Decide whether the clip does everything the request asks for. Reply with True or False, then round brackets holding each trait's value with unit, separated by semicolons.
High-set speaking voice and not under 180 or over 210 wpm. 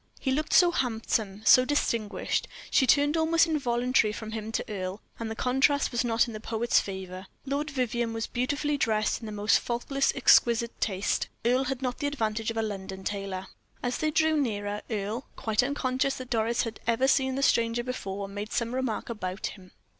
True (235 Hz; 190 wpm)